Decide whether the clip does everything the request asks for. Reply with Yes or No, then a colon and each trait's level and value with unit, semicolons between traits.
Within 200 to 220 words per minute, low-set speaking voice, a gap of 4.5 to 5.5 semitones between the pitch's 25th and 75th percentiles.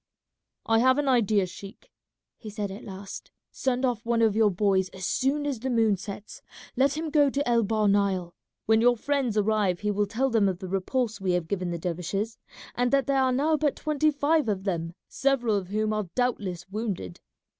No: fast, 205 wpm; high, 215 Hz; average, 4.9 semitones